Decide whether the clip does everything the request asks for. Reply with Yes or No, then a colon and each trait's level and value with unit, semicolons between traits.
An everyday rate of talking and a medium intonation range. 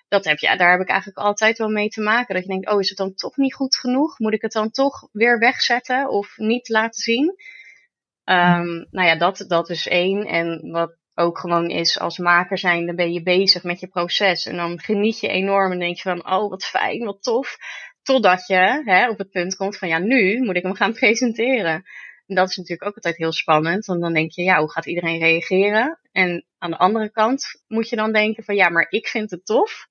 No: fast, 235 wpm; average, 4.1 semitones